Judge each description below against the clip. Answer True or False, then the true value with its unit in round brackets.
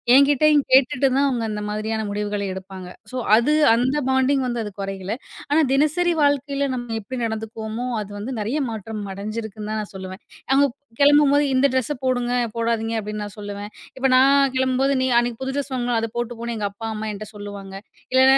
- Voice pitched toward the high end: True (235 Hz)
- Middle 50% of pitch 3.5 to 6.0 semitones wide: True (4.1 semitones)